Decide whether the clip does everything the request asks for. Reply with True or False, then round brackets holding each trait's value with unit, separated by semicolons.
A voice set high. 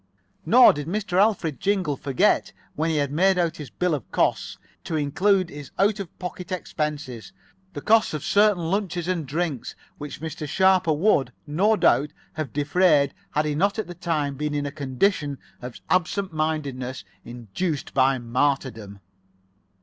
False (155 Hz)